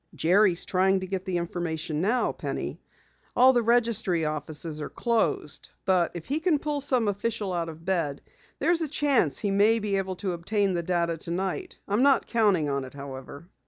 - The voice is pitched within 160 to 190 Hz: Yes, medium, 185 Hz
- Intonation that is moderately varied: No, wide, 5.8 semitones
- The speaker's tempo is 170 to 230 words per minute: Yes, average, 175 wpm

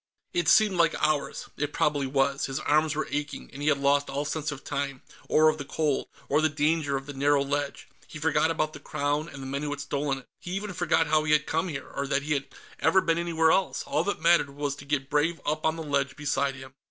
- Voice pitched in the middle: Yes, medium, 145 Hz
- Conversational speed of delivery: No, fast, 250 wpm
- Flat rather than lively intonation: Yes, narrow, 2.0 semitones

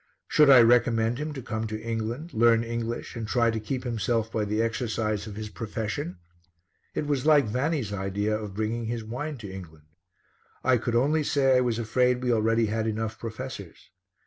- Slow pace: No, average, 185 wpm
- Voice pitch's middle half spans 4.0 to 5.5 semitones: No, narrow, 2.5 semitones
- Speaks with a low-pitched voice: Yes, low, 115 Hz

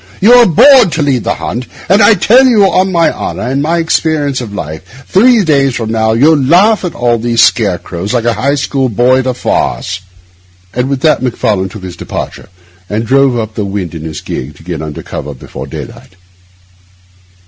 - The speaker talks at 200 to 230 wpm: Yes, fast, 205 wpm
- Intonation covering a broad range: Yes, wide, 7.2 semitones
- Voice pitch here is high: No, low, 130 Hz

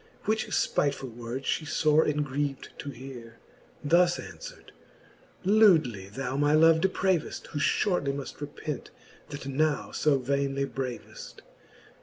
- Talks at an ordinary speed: No, slow, 120 wpm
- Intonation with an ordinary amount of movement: Yes, average, 3.0 semitones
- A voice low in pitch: No, medium, 145 Hz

